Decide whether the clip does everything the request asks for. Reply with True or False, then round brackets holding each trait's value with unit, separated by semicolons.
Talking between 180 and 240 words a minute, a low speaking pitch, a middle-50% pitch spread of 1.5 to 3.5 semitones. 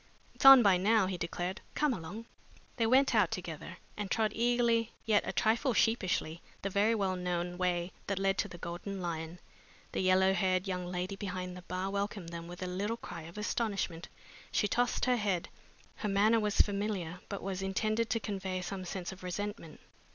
False (190 wpm; 195 Hz; 3.1 semitones)